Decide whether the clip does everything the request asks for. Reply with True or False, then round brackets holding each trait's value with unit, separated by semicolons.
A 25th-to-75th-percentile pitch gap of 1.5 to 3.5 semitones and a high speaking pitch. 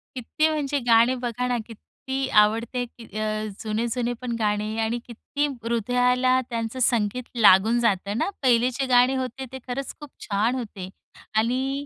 True (2.4 semitones; 240 Hz)